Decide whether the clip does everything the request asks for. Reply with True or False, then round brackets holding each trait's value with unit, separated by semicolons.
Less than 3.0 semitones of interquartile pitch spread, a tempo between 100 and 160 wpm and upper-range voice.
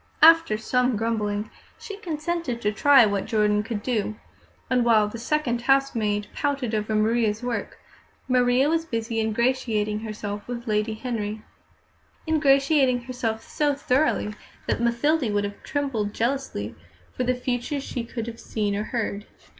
False (4.0 semitones; 145 wpm; 235 Hz)